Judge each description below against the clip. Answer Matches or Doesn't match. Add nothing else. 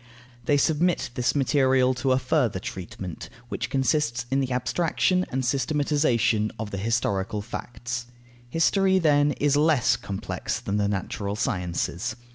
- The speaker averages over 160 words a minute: Doesn't match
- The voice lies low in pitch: Matches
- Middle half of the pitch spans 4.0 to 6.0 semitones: Matches